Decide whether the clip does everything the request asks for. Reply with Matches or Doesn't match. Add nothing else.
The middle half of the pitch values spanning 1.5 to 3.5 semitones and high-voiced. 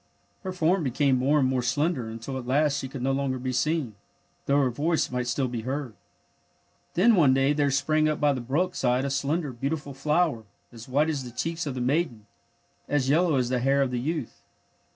Doesn't match